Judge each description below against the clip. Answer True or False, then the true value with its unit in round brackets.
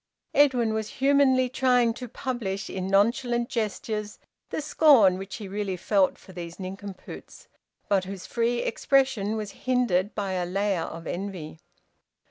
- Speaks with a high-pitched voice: True (210 Hz)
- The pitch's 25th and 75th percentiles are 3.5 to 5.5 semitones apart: True (4.4 semitones)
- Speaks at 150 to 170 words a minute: False (140 wpm)